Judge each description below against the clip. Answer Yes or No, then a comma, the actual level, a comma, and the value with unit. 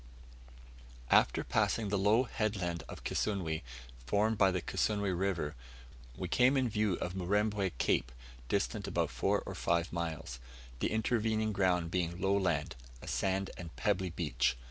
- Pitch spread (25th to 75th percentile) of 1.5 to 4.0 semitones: Yes, average, 3.7 semitones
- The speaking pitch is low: Yes, very low, 95 Hz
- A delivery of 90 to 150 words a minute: Yes, average, 145 wpm